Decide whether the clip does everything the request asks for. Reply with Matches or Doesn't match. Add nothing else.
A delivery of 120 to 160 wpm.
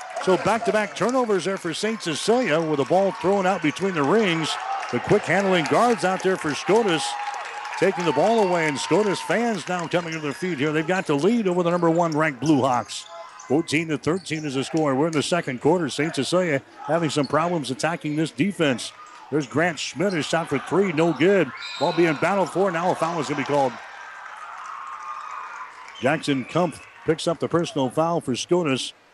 Doesn't match